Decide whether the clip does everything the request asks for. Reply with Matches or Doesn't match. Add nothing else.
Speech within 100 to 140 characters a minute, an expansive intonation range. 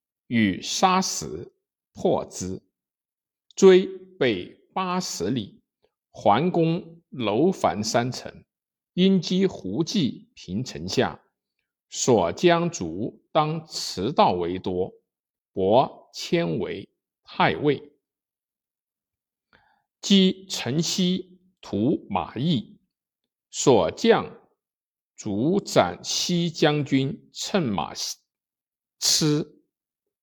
Doesn't match